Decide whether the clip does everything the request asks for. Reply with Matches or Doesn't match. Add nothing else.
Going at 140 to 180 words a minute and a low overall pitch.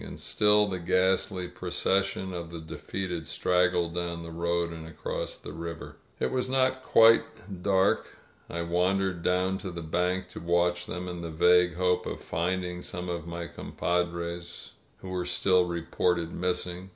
Matches